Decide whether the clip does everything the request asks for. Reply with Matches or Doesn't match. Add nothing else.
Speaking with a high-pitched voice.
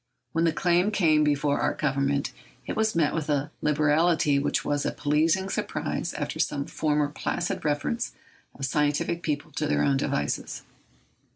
Doesn't match